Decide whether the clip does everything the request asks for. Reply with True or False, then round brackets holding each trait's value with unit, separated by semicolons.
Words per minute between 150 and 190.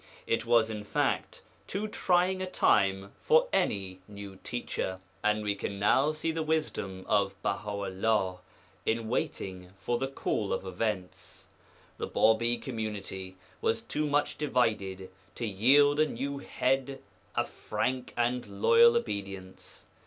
False (140 wpm)